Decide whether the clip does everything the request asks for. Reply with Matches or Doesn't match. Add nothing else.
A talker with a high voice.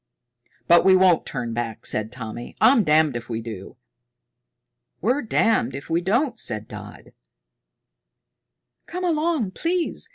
Doesn't match